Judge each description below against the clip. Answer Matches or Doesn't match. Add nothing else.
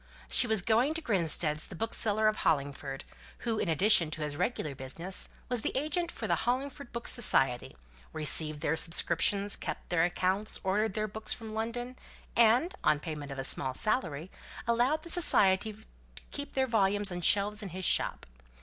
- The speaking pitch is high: Matches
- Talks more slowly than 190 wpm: Matches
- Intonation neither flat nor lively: Doesn't match